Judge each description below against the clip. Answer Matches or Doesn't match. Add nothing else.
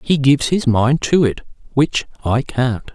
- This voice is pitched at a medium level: Doesn't match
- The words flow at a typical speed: Matches